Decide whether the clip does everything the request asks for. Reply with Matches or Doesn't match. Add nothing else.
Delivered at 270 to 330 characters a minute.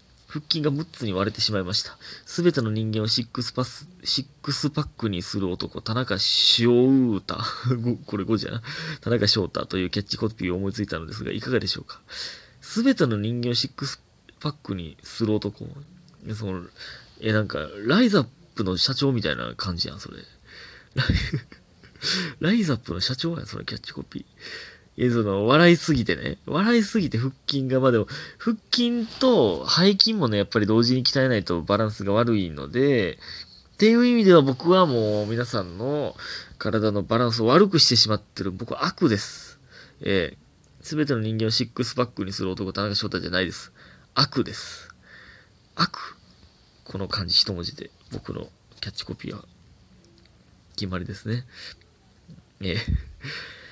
Matches